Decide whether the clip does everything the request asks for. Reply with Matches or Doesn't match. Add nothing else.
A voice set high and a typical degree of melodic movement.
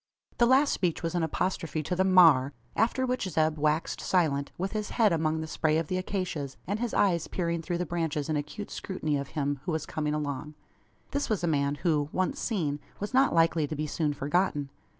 Doesn't match